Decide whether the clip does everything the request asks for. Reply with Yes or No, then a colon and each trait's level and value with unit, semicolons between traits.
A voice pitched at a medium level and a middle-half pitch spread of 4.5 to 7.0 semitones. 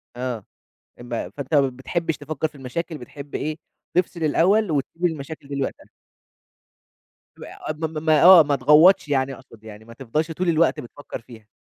No: medium, 145 Hz; average, 3.8 semitones